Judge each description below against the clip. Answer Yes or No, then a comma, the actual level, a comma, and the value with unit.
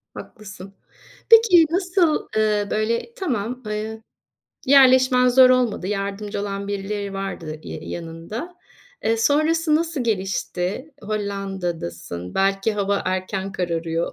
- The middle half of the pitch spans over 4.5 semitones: Yes, average, 5.0 semitones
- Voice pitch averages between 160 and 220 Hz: Yes, high, 210 Hz